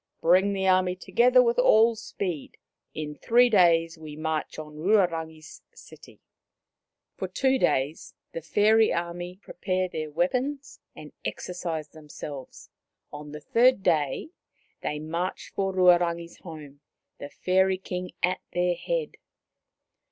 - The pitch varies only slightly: No, average, 3.9 semitones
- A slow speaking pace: Yes, slow, 130 wpm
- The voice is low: No, medium, 175 Hz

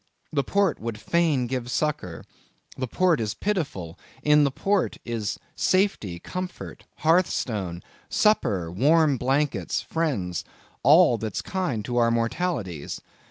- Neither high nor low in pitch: No, low, 130 Hz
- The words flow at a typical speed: No, slow, 120 wpm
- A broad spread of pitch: Yes, wide, 7.6 semitones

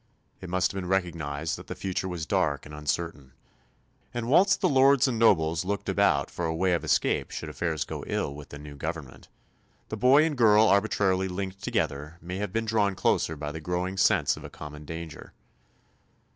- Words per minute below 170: No, average, 195 wpm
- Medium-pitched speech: No, very low, 90 Hz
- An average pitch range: Yes, average, 4.4 semitones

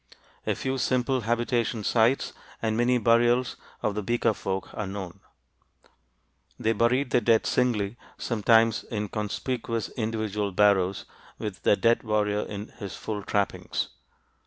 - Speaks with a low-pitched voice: Yes, low, 110 Hz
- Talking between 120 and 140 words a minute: Yes, slow, 135 wpm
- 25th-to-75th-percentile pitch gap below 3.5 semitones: Yes, narrow, 2.5 semitones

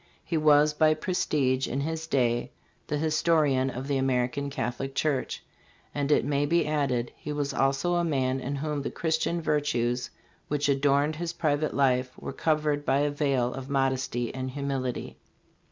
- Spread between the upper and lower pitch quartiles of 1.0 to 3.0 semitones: Yes, narrow, 2.5 semitones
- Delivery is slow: No, average, 165 wpm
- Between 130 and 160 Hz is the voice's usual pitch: Yes, medium, 140 Hz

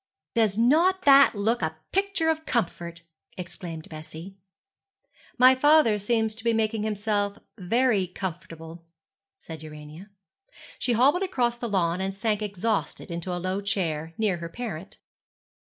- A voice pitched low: No, high, 205 Hz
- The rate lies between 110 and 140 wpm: Yes, slow, 135 wpm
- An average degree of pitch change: No, wide, 5.7 semitones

